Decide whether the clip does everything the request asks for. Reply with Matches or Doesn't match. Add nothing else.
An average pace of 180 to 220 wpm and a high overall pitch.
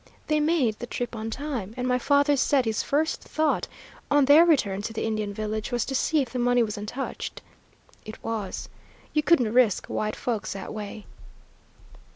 Matches